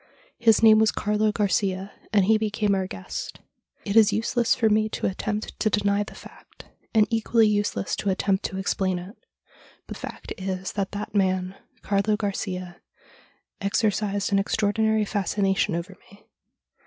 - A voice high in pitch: Yes, high, 205 Hz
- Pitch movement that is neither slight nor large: No, narrow, 1.9 semitones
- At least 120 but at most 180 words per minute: Yes, average, 160 wpm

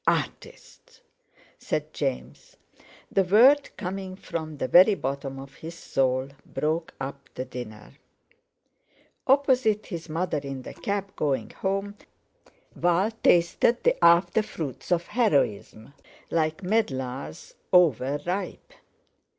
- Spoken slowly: Yes, slow, 110 wpm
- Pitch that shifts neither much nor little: No, wide, 6.4 semitones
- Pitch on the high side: No, medium, 170 Hz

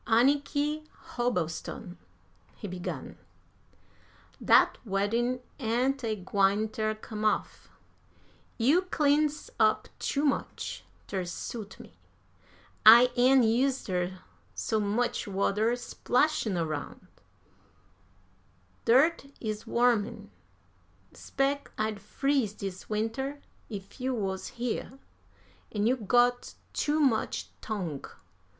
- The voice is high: Yes, high, 225 Hz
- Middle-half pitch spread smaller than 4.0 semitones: No, average, 4.4 semitones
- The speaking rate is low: Yes, slow, 100 wpm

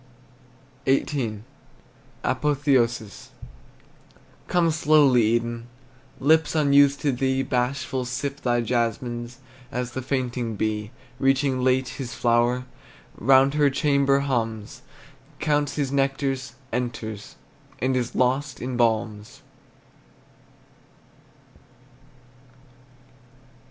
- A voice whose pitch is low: Yes, low, 130 Hz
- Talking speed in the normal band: No, slow, 85 wpm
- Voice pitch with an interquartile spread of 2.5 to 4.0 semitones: Yes, average, 2.8 semitones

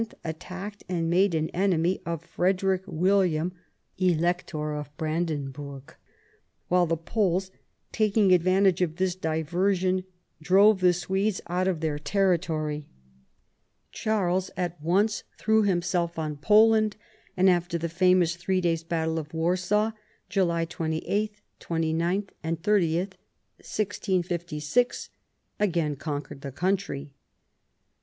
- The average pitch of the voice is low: No, medium, 175 Hz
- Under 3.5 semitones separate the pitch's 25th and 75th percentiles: Yes, average, 2.9 semitones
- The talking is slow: Yes, slow, 110 wpm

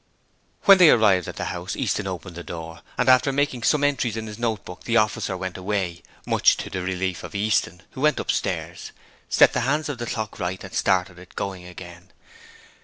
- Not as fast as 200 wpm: No, fast, 205 wpm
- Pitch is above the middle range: No, low, 100 Hz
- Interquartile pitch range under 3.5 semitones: No, average, 4.8 semitones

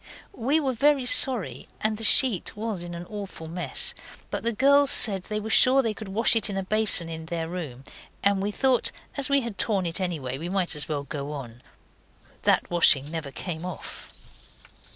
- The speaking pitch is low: No, high, 195 Hz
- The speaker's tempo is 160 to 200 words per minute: Yes, average, 195 wpm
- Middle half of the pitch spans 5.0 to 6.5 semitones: Yes, wide, 5.6 semitones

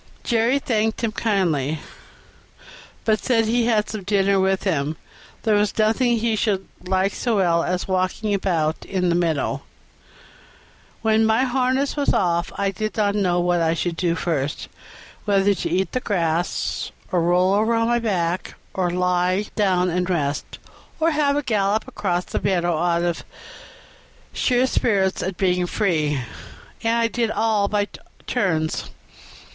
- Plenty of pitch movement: No, average, 4.0 semitones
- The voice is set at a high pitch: Yes, high, 195 Hz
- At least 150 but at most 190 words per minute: Yes, average, 160 wpm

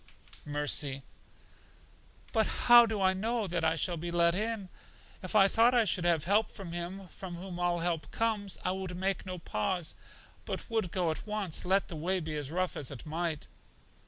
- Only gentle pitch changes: No, average, 3.2 semitones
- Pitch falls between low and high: Yes, medium, 180 Hz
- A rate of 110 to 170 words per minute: No, average, 190 wpm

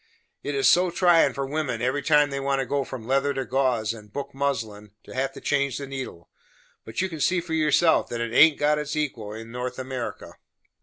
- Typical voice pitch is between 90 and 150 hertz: Yes, low, 135 Hz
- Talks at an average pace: No, fast, 220 wpm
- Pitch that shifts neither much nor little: Yes, average, 3.4 semitones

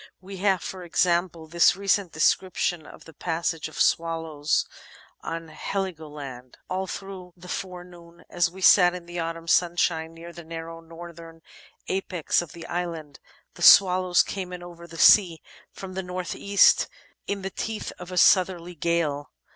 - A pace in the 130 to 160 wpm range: Yes, average, 155 wpm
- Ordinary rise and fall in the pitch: No, narrow, 1.9 semitones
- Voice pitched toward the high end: No, medium, 175 Hz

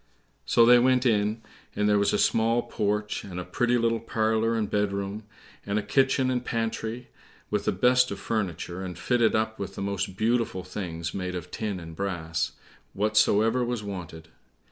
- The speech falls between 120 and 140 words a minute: No, average, 175 wpm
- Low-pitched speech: Yes, low, 105 Hz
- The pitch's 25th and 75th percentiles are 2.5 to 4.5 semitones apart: Yes, average, 3.3 semitones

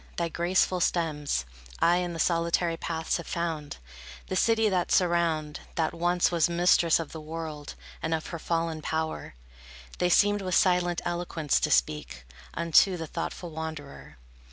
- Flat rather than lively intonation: Yes, narrow, 1.8 semitones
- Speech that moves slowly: No, average, 155 wpm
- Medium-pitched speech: Yes, medium, 170 Hz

